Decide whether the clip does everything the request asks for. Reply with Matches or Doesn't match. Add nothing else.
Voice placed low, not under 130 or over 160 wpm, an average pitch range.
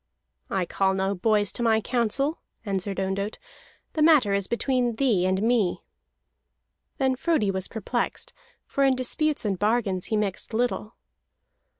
Doesn't match